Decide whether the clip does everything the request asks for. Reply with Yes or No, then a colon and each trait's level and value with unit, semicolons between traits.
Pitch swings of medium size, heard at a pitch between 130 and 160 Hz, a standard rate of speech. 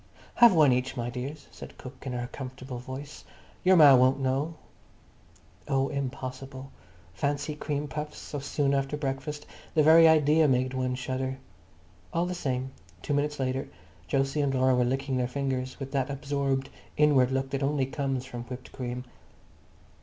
No: narrow, 2.0 semitones; low, 135 Hz; average, 160 wpm